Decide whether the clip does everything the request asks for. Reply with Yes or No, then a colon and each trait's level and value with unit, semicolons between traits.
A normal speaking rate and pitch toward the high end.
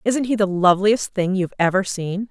No: fast, 210 wpm; high, 195 Hz